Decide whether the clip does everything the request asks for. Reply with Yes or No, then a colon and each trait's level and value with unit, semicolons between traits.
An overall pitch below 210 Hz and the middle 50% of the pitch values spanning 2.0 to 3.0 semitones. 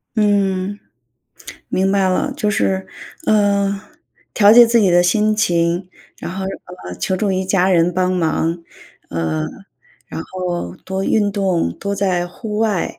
Yes: high, 190 Hz; narrow, 2.4 semitones